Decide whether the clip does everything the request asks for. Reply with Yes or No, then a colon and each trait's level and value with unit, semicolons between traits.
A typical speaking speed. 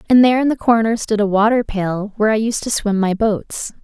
No: fast, 235 wpm